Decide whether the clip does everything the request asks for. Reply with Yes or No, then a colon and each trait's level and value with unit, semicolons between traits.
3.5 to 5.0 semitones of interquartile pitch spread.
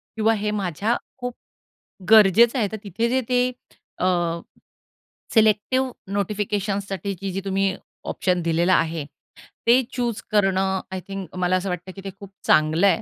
No: average, 2.9 semitones